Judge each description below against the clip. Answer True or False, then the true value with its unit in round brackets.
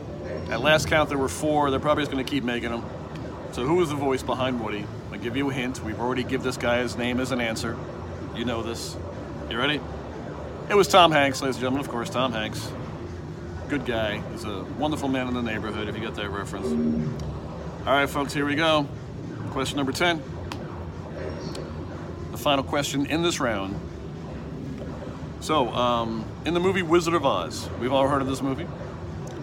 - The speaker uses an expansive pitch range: False (4.9 semitones)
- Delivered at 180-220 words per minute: True (190 wpm)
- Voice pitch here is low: True (125 Hz)